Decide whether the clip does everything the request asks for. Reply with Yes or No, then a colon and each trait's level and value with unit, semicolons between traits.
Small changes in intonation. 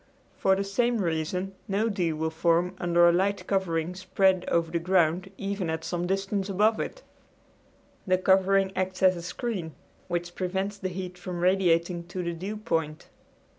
Yes: narrow, 2.1 semitones